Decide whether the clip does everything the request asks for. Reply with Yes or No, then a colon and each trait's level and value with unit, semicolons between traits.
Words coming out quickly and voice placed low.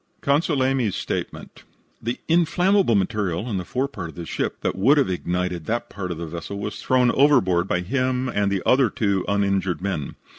No: average, 185 wpm; low, 100 Hz